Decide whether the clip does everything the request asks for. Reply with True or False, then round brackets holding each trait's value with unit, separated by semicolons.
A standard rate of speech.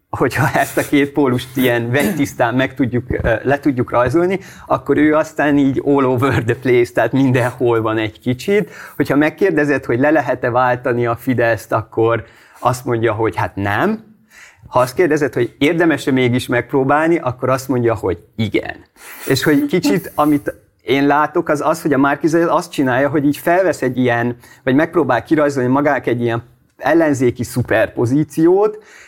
False (160 wpm)